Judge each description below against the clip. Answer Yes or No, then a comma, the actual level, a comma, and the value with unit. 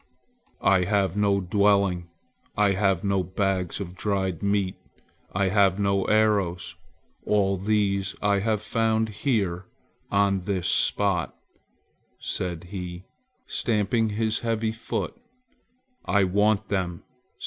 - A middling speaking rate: No, slow, 115 wpm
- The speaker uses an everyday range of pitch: No, narrow, 2.0 semitones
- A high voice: No, low, 100 Hz